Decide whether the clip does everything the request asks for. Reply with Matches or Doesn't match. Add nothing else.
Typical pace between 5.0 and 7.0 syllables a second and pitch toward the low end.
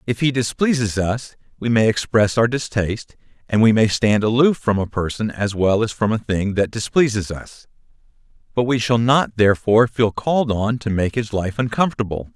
Matches